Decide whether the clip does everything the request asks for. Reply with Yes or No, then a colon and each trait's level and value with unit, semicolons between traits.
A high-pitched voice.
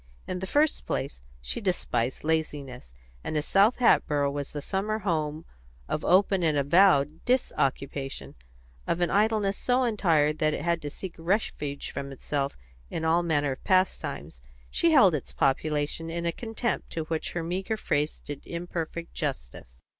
No: medium, 165 Hz